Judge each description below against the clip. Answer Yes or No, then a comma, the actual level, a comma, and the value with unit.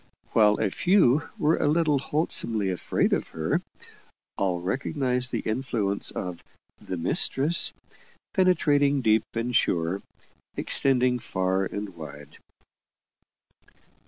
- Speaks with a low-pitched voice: Yes, low, 115 Hz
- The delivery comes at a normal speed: No, slow, 105 wpm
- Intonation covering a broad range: Yes, wide, 7.1 semitones